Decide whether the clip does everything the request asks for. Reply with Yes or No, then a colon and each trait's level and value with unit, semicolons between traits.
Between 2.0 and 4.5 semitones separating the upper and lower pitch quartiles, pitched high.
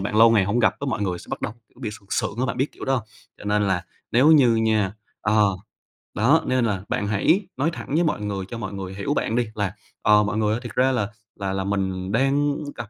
No: average, 4.1 semitones; low, 105 Hz